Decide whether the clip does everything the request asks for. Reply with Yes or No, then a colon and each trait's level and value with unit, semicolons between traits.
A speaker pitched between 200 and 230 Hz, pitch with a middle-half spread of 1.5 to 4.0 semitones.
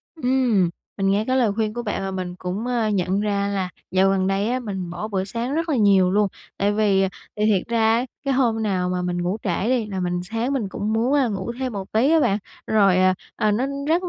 Yes: high, 205 Hz; average, 3.6 semitones